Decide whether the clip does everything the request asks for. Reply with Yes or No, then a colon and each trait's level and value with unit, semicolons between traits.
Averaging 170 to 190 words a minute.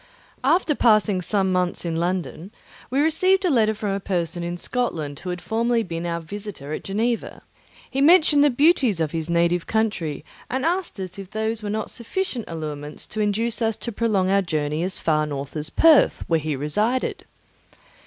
Yes: average, 185 wpm